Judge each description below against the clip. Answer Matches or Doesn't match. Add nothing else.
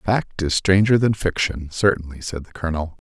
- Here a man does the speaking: Matches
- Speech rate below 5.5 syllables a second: Matches